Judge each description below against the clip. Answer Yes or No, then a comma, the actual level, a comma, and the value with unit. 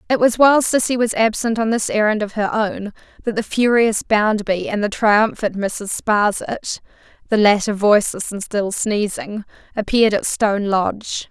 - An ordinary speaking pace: Yes, average, 165 wpm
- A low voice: No, high, 215 Hz